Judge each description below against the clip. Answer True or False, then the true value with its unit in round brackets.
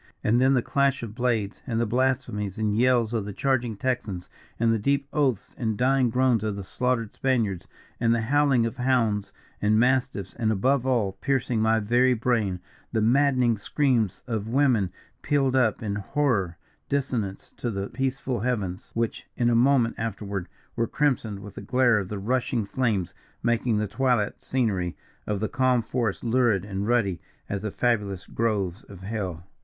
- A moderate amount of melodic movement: True (3.7 semitones)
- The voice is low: True (115 Hz)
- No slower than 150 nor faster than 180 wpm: True (170 wpm)